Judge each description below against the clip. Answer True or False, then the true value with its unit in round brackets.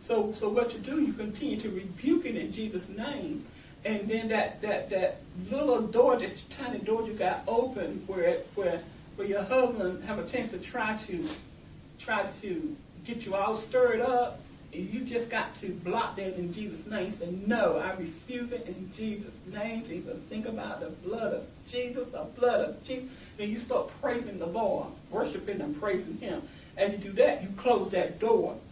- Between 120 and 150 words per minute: False (190 wpm)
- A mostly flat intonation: False (4.3 semitones)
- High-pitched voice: True (220 Hz)